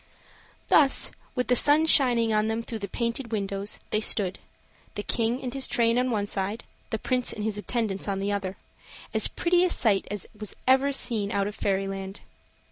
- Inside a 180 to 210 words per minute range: Yes, average, 190 wpm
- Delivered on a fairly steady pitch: No, average, 3.8 semitones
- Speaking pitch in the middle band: No, high, 220 Hz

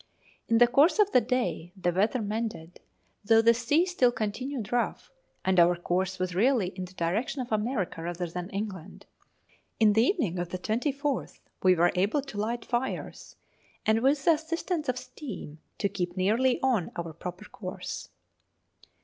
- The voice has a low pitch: No, high, 215 Hz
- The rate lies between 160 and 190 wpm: Yes, average, 165 wpm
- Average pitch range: No, wide, 5.7 semitones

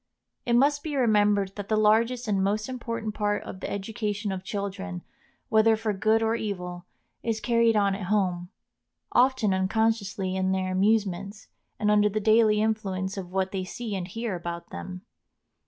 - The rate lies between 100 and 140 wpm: No, average, 170 wpm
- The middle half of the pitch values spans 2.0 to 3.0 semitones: Yes, narrow, 2.6 semitones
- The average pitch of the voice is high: Yes, high, 210 Hz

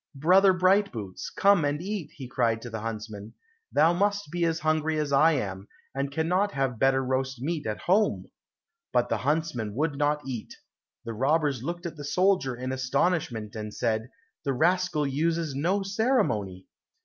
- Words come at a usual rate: Yes, average, 165 wpm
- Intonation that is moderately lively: No, wide, 5.8 semitones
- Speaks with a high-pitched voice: No, medium, 145 Hz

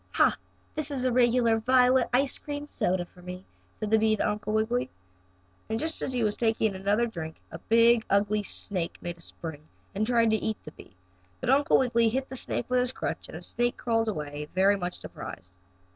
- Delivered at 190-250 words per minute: Yes, fast, 205 wpm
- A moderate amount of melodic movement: Yes, average, 4.3 semitones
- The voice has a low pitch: No, high, 220 Hz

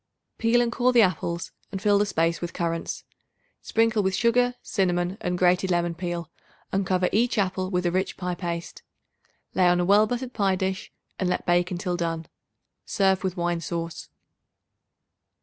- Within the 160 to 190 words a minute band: Yes, average, 170 wpm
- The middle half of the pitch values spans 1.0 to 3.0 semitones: Yes, narrow, 2.6 semitones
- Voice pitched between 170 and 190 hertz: Yes, medium, 185 Hz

